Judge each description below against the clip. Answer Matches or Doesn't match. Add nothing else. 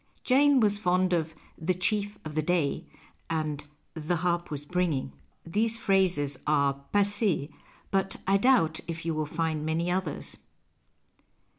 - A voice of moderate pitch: Matches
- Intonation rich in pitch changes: Doesn't match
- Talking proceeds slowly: Doesn't match